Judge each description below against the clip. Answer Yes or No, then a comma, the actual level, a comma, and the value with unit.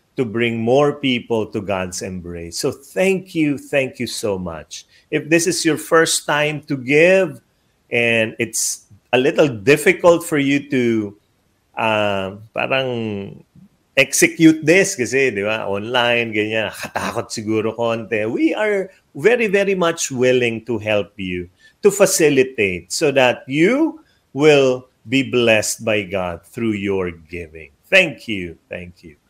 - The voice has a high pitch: No, low, 125 Hz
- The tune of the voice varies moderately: No, wide, 6.3 semitones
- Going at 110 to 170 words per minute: Yes, slow, 135 wpm